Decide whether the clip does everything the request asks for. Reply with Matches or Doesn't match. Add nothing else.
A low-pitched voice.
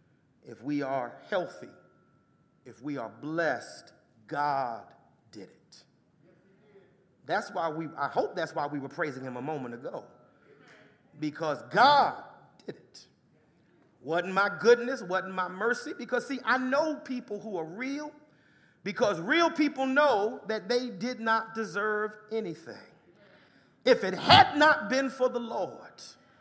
Doesn't match